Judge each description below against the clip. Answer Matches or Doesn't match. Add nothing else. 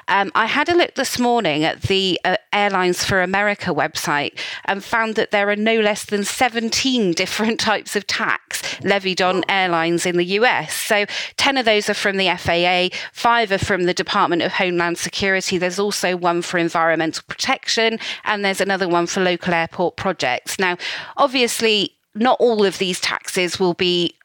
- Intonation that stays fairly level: Doesn't match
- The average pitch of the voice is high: Matches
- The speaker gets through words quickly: Doesn't match